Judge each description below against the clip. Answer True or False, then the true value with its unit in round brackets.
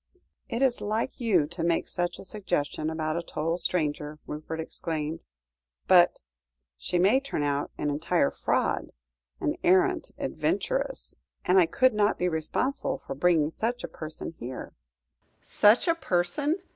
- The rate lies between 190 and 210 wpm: False (145 wpm)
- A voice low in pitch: False (175 Hz)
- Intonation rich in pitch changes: True (5.7 semitones)